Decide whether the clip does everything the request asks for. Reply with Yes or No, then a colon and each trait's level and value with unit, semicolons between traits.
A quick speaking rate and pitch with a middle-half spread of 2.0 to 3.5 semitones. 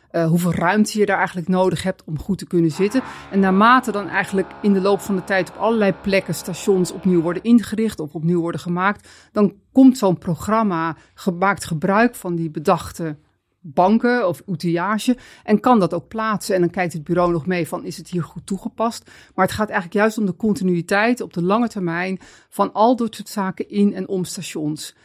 Yes: fast, 205 wpm; average, 3.2 semitones